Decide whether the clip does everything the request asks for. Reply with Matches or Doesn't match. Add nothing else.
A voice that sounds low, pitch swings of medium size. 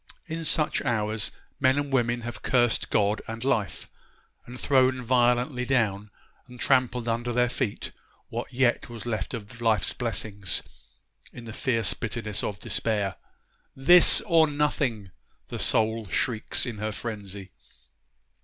Matches